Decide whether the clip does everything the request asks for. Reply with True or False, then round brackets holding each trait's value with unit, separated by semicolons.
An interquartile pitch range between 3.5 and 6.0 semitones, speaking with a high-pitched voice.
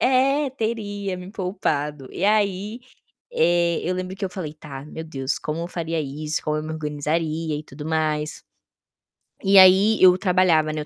False (4.2 semitones; 170 Hz)